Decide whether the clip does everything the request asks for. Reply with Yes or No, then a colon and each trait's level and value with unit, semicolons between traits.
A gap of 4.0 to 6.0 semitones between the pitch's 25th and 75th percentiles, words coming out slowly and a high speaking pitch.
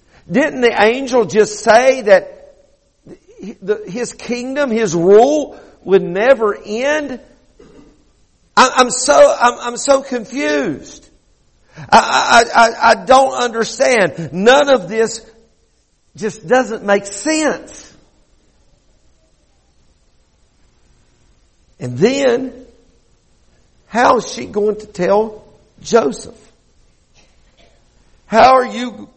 Yes: average, 4.6 semitones; slow, 85 wpm; high, 225 Hz